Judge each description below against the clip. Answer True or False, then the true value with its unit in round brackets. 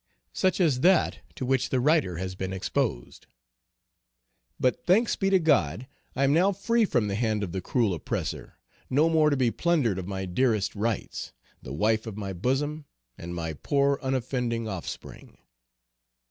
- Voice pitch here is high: False (125 Hz)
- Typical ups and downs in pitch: False (7.4 semitones)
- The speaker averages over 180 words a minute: False (165 wpm)